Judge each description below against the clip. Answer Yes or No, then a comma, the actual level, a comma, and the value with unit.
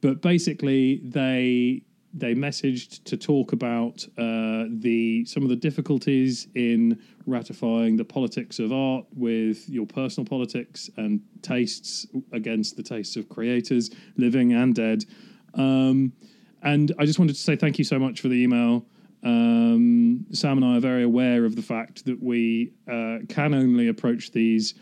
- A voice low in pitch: Yes, low, 130 Hz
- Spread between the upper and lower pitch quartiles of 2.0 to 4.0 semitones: No, average, 4.5 semitones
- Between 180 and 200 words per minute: No, average, 155 wpm